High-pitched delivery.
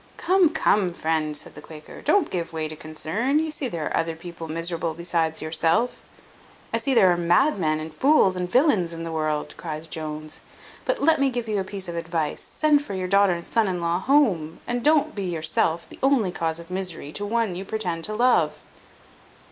No: medium, 180 Hz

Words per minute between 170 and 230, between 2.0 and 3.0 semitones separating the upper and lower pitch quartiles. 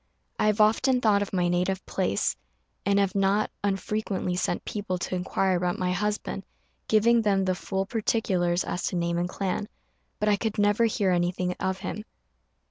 Yes: average, 175 wpm; narrow, 2.6 semitones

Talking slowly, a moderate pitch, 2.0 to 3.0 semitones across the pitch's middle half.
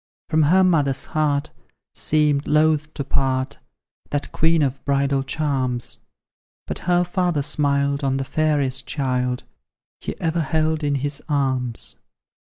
Yes: slow, 130 wpm; medium, 145 Hz; narrow, 2.4 semitones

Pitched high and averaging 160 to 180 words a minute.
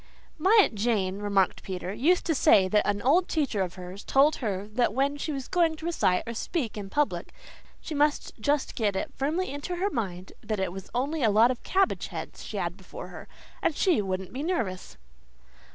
No: high, 245 Hz; fast, 205 wpm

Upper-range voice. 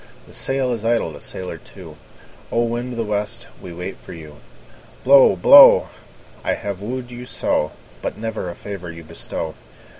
No: low, 105 Hz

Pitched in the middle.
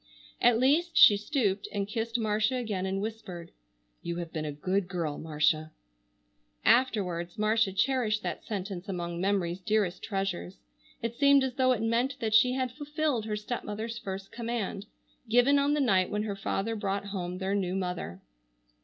No: high, 210 Hz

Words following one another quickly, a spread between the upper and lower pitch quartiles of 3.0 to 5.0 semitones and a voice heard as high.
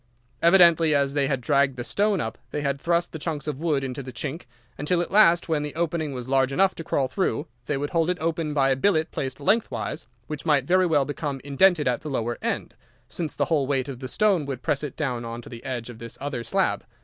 No: fast, 245 wpm; average, 3.9 semitones; medium, 145 Hz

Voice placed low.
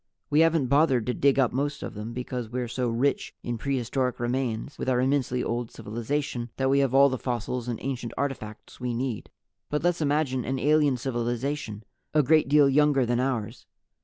Yes: low, 130 Hz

